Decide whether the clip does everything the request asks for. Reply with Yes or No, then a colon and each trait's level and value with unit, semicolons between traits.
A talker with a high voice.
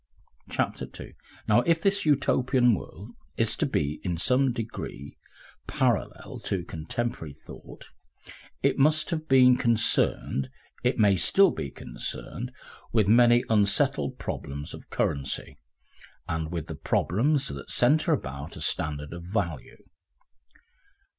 No: low, 110 Hz